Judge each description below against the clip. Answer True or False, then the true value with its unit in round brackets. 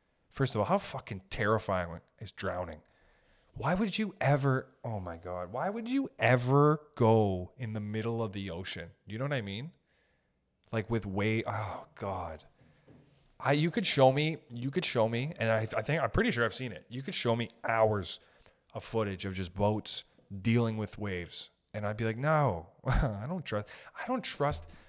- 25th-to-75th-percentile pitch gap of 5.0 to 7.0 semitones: True (5.3 semitones)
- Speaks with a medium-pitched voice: False (110 Hz)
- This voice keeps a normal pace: True (190 wpm)